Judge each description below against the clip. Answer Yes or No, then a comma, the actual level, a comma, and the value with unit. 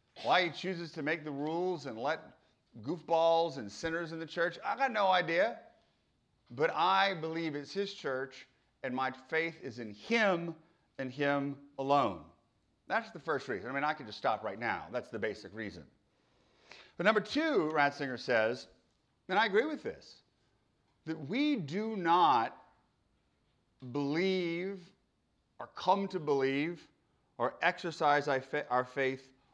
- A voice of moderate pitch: Yes, medium, 165 Hz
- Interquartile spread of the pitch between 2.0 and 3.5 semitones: No, average, 4.5 semitones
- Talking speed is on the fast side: No, average, 150 wpm